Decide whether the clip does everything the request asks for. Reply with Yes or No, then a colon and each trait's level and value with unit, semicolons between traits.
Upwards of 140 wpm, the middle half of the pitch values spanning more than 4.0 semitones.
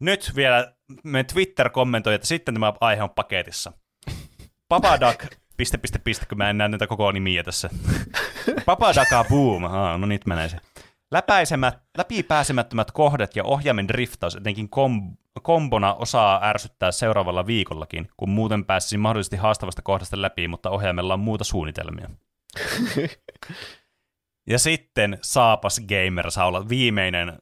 No: average, 135 wpm; average, 4.4 semitones